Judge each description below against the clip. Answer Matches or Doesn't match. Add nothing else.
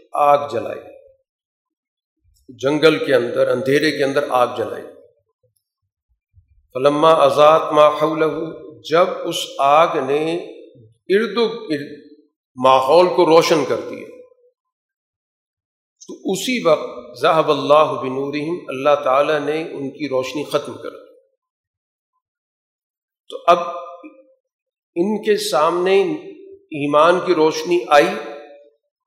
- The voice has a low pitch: Doesn't match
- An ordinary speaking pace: Doesn't match